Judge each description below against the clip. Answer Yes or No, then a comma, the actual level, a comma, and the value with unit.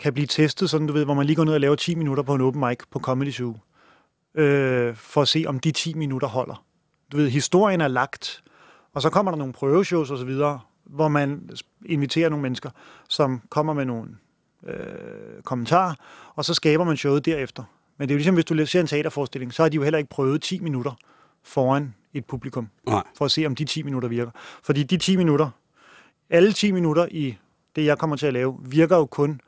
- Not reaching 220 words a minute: No, fast, 225 wpm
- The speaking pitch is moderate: Yes, medium, 145 Hz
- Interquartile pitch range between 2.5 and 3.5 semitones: Yes, average, 2.9 semitones